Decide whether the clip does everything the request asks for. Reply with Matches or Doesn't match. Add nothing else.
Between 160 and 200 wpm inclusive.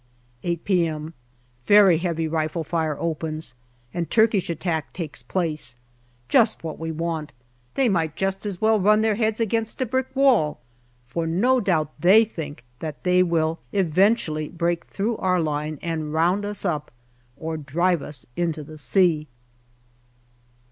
Doesn't match